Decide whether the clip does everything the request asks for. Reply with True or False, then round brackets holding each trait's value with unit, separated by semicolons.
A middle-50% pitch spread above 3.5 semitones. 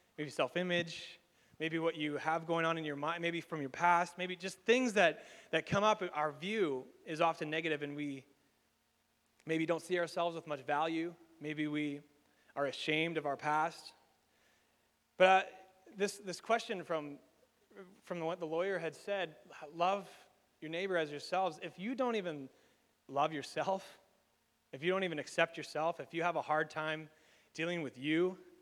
False (3.0 semitones)